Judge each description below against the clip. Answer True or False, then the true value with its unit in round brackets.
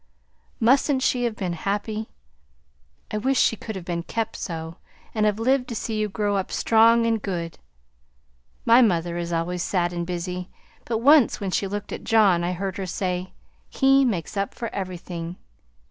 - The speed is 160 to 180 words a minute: True (175 wpm)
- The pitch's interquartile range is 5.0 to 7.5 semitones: False (4.3 semitones)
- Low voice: False (200 Hz)